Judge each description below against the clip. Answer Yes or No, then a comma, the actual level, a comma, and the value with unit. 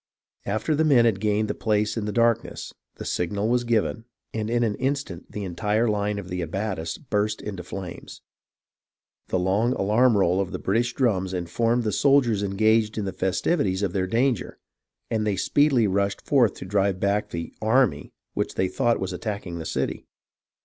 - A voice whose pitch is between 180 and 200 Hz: No, low, 105 Hz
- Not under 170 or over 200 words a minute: Yes, average, 180 wpm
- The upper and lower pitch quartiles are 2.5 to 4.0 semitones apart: Yes, average, 3.4 semitones